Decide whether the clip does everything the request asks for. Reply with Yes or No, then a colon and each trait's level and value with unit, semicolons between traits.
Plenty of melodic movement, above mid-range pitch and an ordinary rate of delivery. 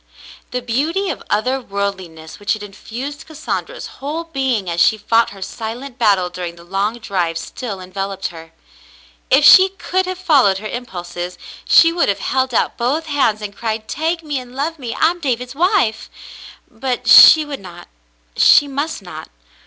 Yes: wide, 6.8 semitones; high, 235 Hz; average, 175 wpm